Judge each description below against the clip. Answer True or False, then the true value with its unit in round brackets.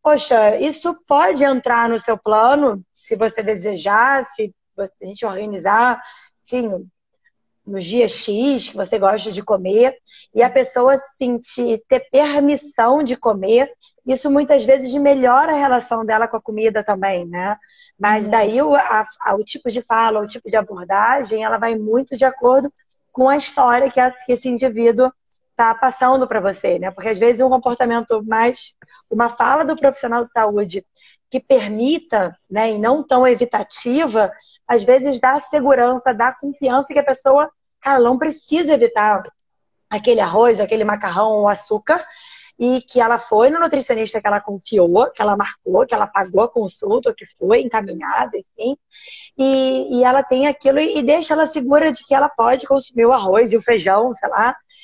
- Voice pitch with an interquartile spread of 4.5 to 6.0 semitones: False (3.9 semitones)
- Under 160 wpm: False (165 wpm)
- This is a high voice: True (245 Hz)